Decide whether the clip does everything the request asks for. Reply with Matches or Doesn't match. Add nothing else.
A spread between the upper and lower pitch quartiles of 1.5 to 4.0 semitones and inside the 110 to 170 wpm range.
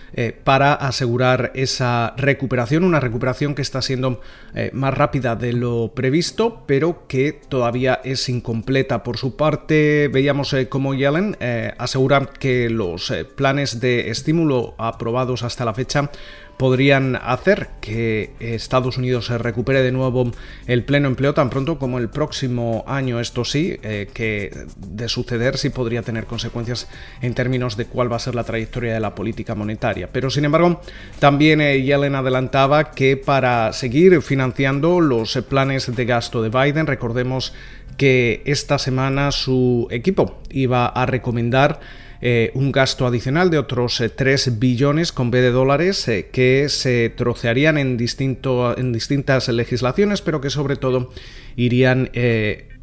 Matches